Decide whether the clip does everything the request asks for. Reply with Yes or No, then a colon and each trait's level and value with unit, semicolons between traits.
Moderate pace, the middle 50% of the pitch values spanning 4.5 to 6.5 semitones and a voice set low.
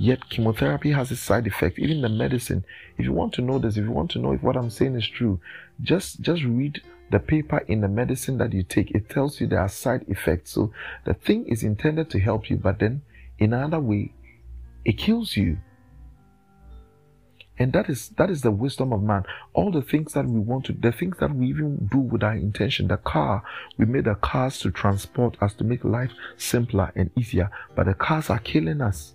No: fast, 220 wpm; average, 5.0 semitones; low, 120 Hz